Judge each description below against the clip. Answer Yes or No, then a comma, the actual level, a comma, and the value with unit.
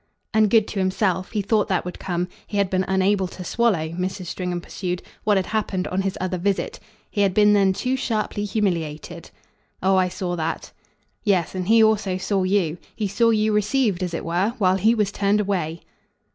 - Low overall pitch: No, high, 190 Hz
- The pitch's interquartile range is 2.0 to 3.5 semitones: Yes, narrow, 2.5 semitones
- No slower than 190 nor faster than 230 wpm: Yes, average, 200 wpm